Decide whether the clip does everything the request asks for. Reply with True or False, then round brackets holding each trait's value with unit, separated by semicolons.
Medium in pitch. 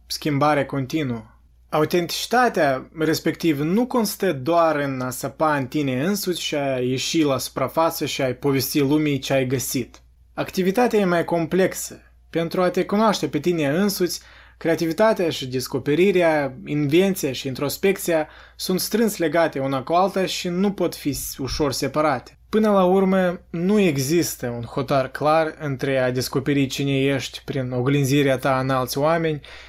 True (150 Hz)